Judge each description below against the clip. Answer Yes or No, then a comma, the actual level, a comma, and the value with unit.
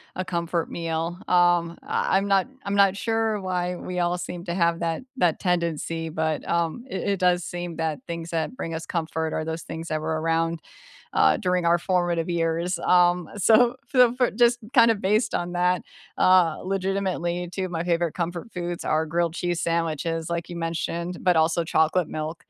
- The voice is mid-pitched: Yes, medium, 175 Hz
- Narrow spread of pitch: Yes, narrow, 1.7 semitones